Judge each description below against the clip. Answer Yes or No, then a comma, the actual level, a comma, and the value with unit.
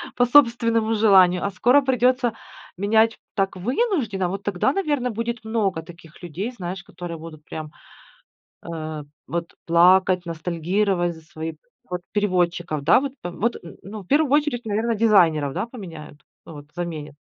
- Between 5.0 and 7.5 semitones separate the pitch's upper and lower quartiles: Yes, average, 5.3 semitones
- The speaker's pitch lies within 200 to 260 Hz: No, high, 190 Hz